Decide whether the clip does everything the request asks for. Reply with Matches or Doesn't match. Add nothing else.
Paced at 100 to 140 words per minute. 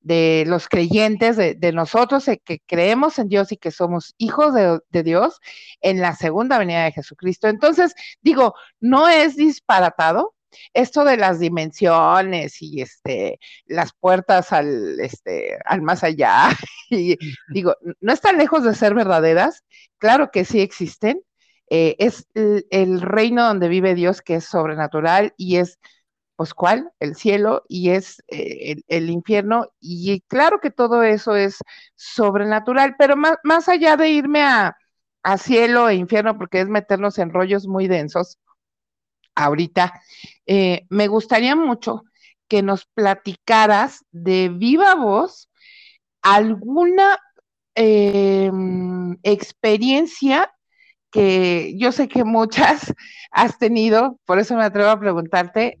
Matches